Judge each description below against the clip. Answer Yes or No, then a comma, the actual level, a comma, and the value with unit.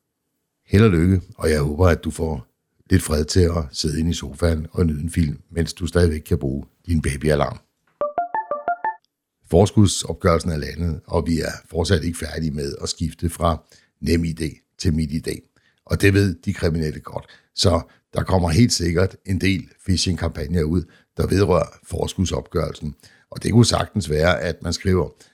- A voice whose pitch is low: Yes, very low, 85 Hz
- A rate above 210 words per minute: No, average, 170 wpm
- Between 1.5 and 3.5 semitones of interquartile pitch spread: Yes, average, 2.9 semitones